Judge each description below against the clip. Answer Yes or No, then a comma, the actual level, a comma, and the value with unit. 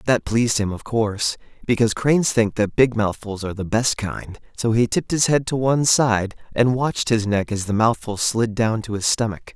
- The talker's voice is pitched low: Yes, low, 110 Hz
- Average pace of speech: No, fast, 220 wpm